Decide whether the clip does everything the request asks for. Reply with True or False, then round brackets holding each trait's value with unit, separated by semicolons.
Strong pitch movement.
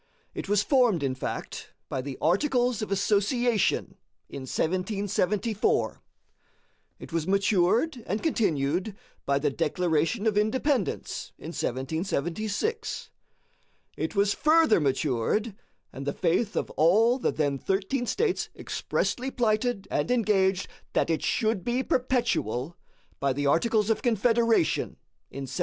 True (6.5 semitones)